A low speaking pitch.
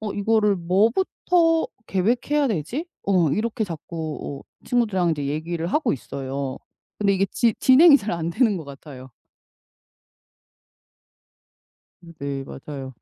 No: medium, 185 Hz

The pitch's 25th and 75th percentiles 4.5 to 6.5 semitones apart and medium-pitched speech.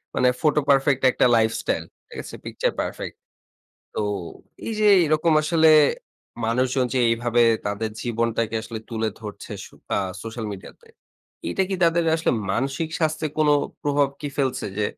No: average, 5.2 semitones; low, 130 Hz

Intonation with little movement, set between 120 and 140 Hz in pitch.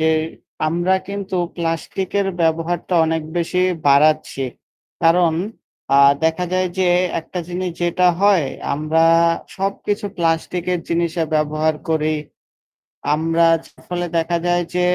No: narrow, 2.0 semitones; medium, 170 Hz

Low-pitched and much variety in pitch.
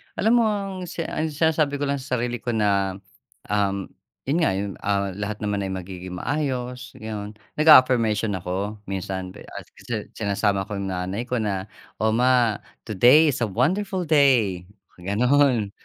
Yes: low, 110 Hz; wide, 5.7 semitones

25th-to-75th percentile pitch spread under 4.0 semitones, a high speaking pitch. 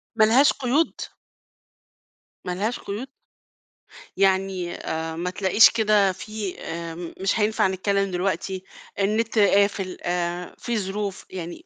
Yes: average, 3.0 semitones; high, 195 Hz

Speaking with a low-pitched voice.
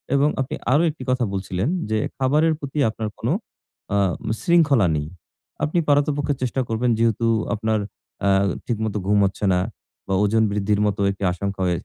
Yes: low, 115 Hz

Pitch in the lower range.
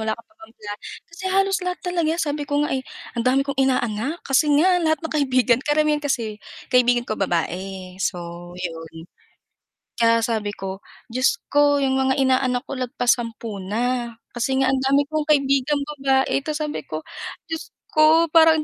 No: very high, 265 Hz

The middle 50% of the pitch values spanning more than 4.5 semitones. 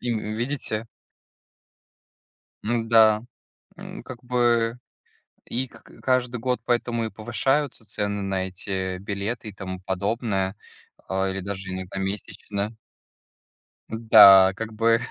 No: average, 3.4 semitones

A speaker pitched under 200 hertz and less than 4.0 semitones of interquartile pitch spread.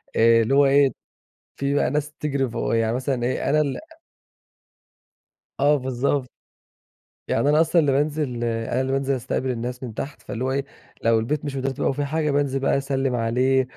Yes: low, 135 Hz; narrow, 2.5 semitones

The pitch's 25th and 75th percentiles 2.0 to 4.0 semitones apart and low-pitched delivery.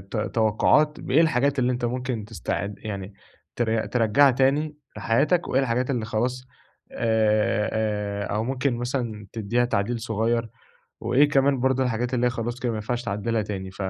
Yes: average, 3.0 semitones; low, 120 Hz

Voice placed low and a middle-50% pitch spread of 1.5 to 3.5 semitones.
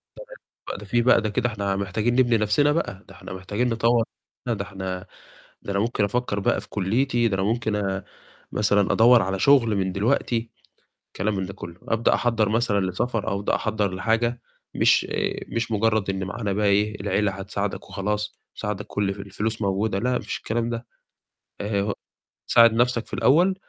Yes: low, 105 Hz; average, 3.0 semitones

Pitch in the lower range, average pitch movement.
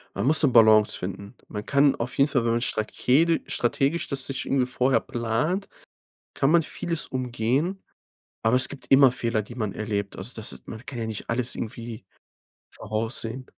Yes: low, 120 Hz; average, 3.6 semitones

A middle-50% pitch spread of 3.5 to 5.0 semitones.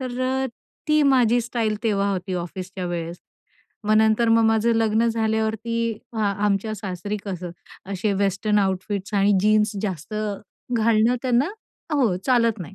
No: average, 2.7 semitones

